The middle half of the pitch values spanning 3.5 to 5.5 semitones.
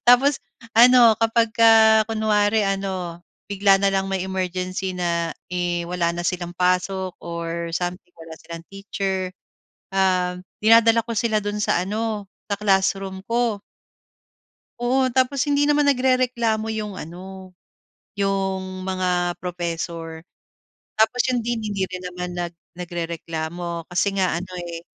Yes: average, 3.8 semitones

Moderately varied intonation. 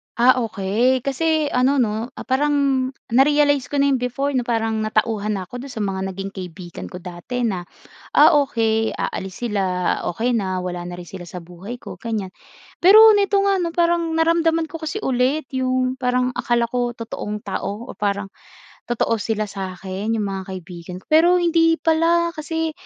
No: wide, 6.6 semitones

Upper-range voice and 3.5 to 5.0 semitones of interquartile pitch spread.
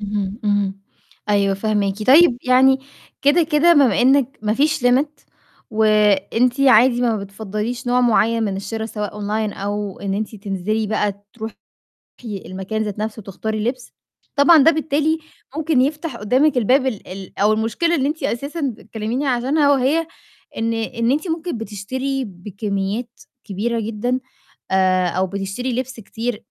Yes: high, 225 Hz; average, 4.4 semitones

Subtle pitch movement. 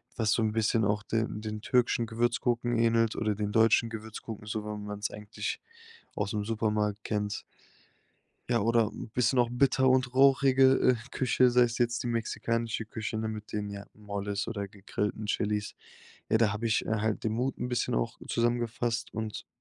Yes: narrow, 2.1 semitones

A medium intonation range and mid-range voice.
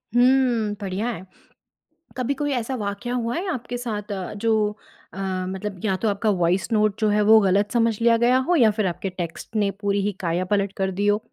No: average, 3.0 semitones; high, 210 Hz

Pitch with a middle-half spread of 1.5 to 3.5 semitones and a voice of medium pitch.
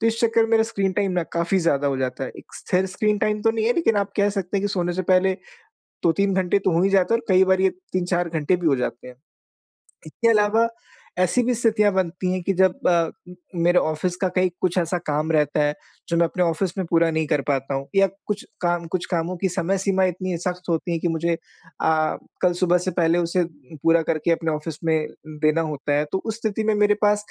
Yes: average, 3.2 semitones; medium, 180 Hz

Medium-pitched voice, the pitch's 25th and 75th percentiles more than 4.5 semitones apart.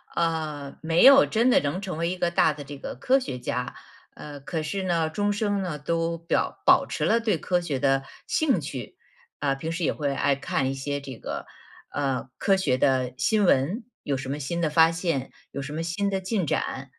Yes: medium, 160 Hz; average, 4.9 semitones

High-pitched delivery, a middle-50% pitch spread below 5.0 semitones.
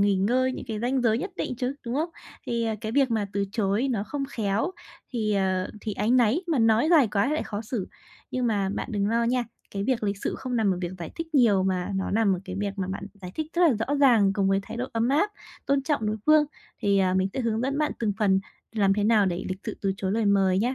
Yes: high, 220 Hz; average, 4.3 semitones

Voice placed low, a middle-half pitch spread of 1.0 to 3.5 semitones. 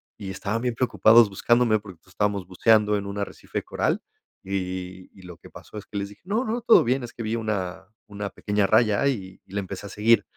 Yes: low, 105 Hz; average, 3.0 semitones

